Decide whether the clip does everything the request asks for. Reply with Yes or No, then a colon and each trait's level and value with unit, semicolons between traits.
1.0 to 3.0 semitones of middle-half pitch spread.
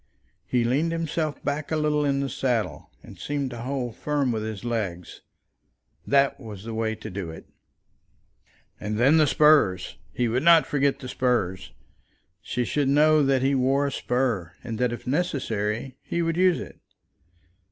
No: average, 4.7 semitones